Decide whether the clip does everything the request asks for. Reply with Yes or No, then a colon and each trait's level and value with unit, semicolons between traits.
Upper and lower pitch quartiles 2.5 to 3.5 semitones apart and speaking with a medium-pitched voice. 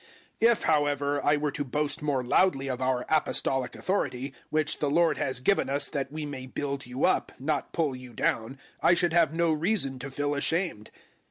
Yes: average, 2.9 semitones; medium, 145 Hz